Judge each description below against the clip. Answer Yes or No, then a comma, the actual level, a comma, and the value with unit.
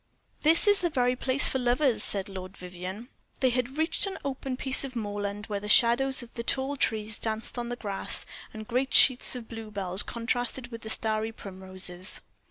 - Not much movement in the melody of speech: No, average, 4.0 semitones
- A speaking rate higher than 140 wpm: Yes, average, 180 wpm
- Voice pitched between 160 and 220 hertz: No, high, 235 Hz